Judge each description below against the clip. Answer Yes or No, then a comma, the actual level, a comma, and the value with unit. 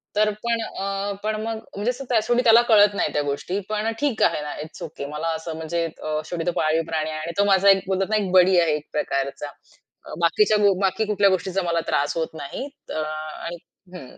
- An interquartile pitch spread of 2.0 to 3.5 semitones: No, average, 5.1 semitones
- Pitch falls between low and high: Yes, medium, 180 Hz